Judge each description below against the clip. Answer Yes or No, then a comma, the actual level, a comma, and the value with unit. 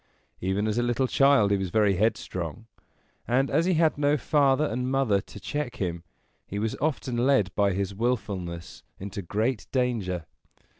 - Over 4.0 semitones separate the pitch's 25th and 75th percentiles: Yes, wide, 5.4 semitones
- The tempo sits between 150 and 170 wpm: Yes, average, 165 wpm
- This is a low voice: Yes, low, 110 Hz